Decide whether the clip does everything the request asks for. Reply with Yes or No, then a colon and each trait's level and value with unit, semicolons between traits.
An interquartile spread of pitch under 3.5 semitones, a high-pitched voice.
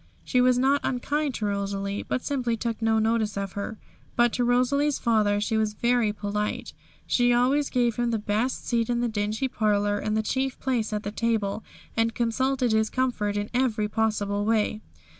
Yes: average, 2.9 semitones; high, 225 Hz